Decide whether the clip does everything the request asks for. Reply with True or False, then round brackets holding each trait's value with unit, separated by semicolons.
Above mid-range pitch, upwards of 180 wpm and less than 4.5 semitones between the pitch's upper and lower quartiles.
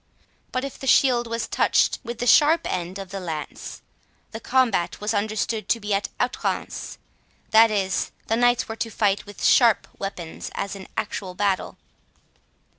False (215 Hz; 165 wpm; 3.3 semitones)